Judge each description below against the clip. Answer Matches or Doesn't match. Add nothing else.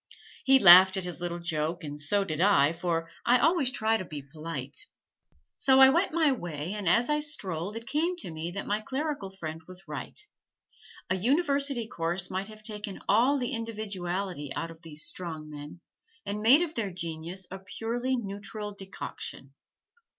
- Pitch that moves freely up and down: Matches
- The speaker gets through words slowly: Doesn't match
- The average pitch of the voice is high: Matches